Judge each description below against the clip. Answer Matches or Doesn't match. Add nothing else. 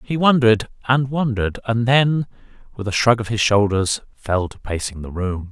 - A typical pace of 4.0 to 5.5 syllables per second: Matches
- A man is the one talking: Matches